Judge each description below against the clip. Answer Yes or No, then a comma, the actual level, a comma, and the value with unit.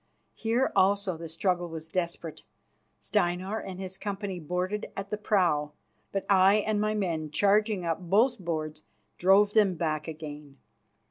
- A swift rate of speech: No, average, 145 wpm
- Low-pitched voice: No, medium, 185 Hz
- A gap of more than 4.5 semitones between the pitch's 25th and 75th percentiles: No, average, 3.8 semitones